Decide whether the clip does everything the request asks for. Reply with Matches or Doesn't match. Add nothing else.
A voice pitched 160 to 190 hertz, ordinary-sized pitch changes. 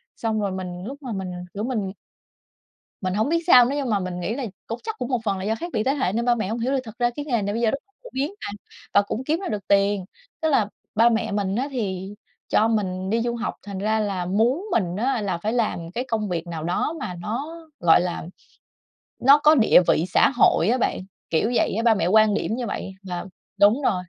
Doesn't match